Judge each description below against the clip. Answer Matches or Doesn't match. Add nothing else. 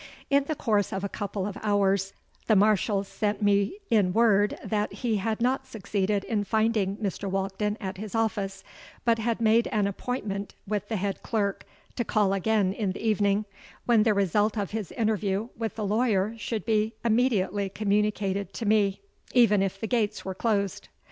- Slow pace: Doesn't match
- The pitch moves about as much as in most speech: Doesn't match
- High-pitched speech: Matches